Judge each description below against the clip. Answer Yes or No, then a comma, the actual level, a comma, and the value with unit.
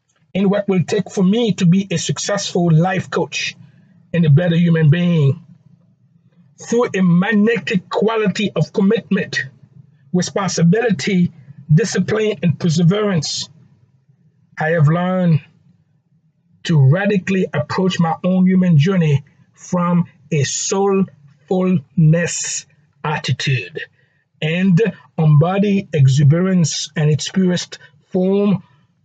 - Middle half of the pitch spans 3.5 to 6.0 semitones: Yes, average, 3.8 semitones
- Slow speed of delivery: Yes, slow, 100 wpm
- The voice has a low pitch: No, medium, 165 Hz